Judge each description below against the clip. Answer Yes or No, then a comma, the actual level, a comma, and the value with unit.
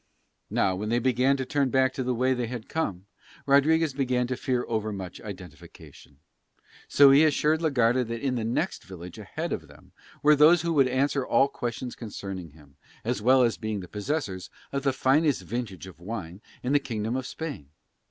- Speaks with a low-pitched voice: Yes, low, 125 Hz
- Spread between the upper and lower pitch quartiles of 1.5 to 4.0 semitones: No, average, 4.7 semitones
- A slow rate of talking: No, average, 190 wpm